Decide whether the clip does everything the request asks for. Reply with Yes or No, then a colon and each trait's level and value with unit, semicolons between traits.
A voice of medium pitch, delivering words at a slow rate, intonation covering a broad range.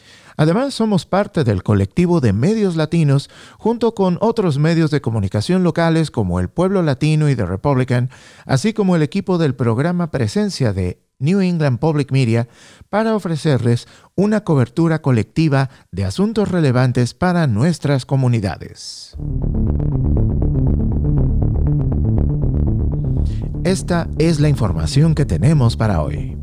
Yes: medium, 145 Hz; slow, 120 wpm; wide, 7.0 semitones